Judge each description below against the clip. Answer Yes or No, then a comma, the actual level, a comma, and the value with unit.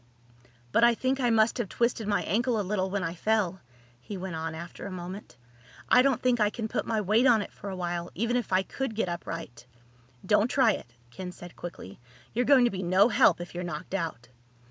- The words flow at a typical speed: No, fast, 225 wpm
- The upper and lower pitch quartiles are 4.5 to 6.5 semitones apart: Yes, average, 4.9 semitones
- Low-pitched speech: No, high, 200 Hz